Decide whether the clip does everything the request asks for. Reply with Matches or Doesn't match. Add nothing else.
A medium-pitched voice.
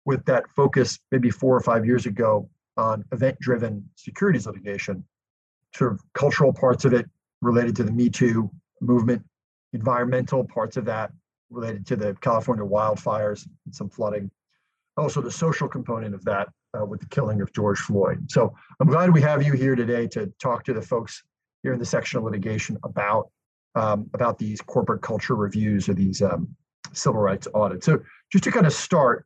Doesn't match